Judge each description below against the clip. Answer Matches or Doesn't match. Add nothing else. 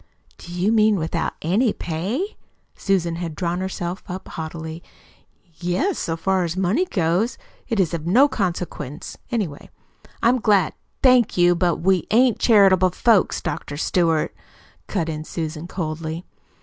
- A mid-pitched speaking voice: Matches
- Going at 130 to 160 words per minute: Matches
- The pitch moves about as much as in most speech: Matches